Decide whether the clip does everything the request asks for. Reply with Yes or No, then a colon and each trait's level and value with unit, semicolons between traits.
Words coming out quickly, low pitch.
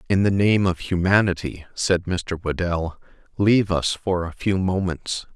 No: average, 155 wpm; very low, 90 Hz